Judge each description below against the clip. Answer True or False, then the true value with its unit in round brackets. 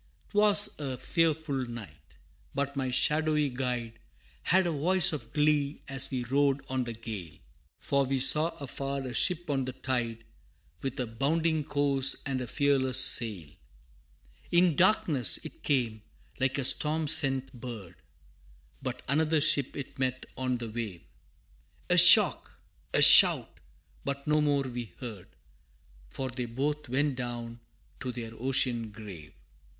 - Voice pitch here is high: False (135 Hz)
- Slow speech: False (145 wpm)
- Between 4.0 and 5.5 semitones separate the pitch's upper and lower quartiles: False (3.4 semitones)